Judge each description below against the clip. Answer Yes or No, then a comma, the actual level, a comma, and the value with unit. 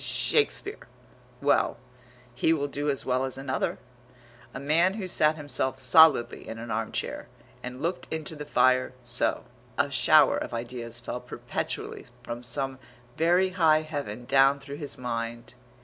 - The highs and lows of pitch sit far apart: No, average, 4.1 semitones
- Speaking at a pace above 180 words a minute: No, average, 150 wpm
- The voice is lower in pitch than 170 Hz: Yes, low, 135 Hz